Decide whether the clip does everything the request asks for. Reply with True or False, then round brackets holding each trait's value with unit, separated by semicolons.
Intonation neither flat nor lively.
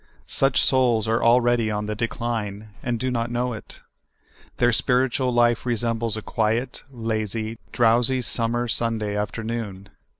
False (1.8 semitones)